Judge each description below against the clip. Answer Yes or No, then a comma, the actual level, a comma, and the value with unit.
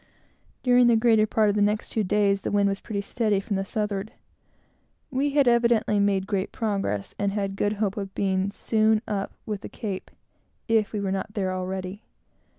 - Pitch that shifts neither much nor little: No, narrow, 2.0 semitones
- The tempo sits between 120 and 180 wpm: No, average, 190 wpm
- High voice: Yes, high, 205 Hz